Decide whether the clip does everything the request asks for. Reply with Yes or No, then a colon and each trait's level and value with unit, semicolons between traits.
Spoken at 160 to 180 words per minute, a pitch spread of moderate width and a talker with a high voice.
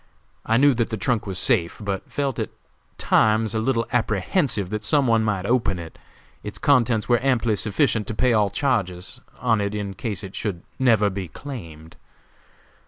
No: average, 175 wpm; average, 3.6 semitones; low, 110 Hz